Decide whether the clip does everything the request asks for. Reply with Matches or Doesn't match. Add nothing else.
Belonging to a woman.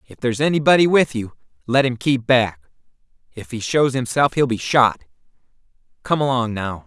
Doesn't match